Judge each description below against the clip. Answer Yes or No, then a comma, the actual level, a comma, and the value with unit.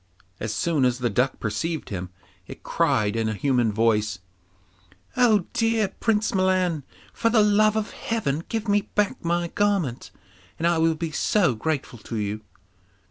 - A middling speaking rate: Yes, average, 160 wpm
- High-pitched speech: No, medium, 165 Hz